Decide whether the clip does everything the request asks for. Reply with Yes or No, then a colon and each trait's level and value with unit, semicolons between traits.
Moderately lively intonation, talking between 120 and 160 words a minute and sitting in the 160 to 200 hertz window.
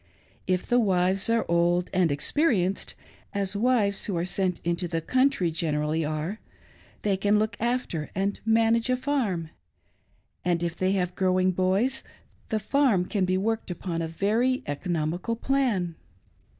Yes: average, 4.6 semitones; average, 155 wpm; high, 190 Hz